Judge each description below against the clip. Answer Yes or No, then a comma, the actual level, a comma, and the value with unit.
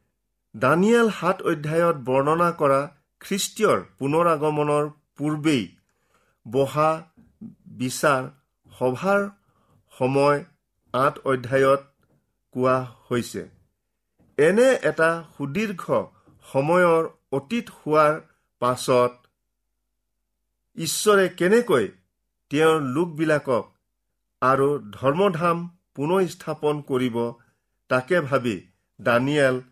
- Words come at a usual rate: No, slow, 70 wpm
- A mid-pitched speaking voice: Yes, medium, 145 Hz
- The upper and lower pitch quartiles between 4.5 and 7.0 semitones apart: Yes, average, 5.1 semitones